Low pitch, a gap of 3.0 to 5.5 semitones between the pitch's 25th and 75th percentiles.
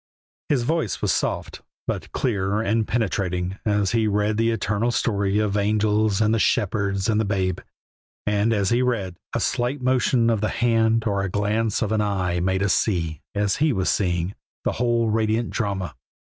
No: low, 105 Hz; narrow, 2.5 semitones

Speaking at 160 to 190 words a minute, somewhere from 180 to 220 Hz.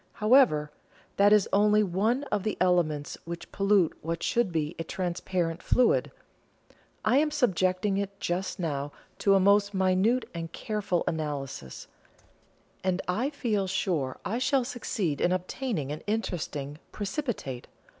No: slow, 135 wpm; high, 190 Hz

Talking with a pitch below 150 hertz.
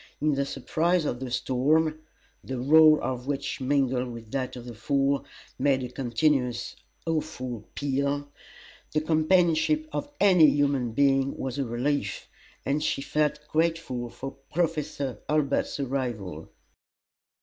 Yes: medium, 140 Hz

